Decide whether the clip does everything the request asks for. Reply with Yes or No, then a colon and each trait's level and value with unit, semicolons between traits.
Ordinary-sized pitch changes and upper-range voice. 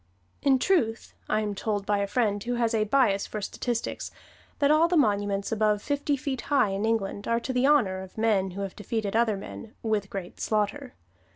Yes: average, 3.7 semitones; high, 220 Hz